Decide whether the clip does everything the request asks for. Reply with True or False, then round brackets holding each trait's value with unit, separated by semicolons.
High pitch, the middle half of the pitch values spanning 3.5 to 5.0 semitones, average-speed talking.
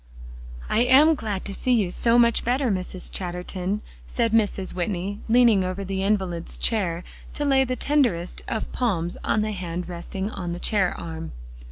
True (195 Hz; 4.4 semitones; 170 wpm)